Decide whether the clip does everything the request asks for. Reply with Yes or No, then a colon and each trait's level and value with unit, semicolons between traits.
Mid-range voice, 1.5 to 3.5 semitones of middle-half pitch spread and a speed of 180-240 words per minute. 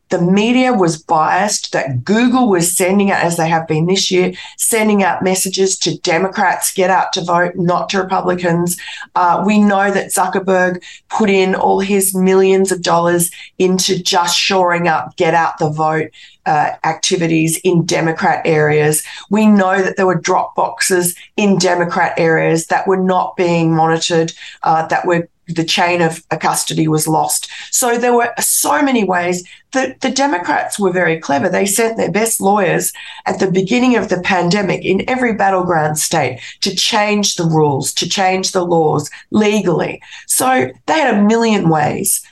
No: medium, 180 Hz; average, 2.8 semitones; average, 170 wpm